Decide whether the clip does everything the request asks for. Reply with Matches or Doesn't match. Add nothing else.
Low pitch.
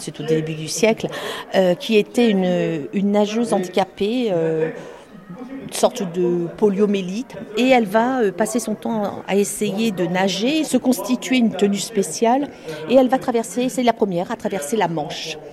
Doesn't match